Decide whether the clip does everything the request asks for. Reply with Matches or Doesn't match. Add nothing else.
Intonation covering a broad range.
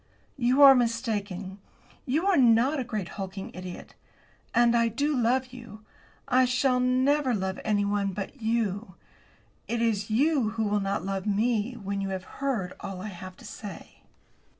Doesn't match